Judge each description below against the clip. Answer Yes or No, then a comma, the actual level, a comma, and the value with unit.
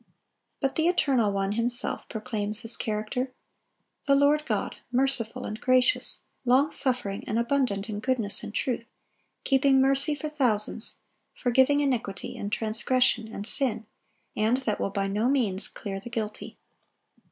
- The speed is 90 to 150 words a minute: Yes, average, 140 wpm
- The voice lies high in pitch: Yes, high, 240 Hz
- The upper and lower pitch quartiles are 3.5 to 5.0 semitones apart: Yes, average, 4.0 semitones